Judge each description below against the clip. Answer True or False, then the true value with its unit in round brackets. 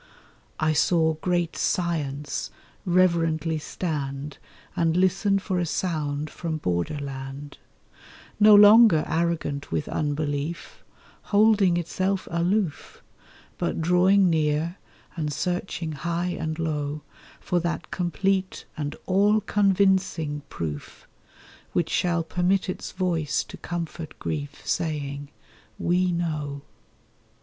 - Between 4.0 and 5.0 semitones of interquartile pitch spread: False (3.5 semitones)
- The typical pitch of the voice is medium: True (165 Hz)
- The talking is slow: True (105 wpm)